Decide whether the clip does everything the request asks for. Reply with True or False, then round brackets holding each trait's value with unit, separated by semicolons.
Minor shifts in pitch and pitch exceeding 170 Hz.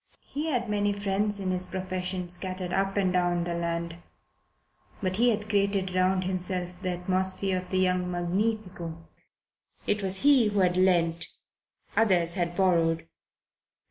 True (2.0 semitones; 185 Hz)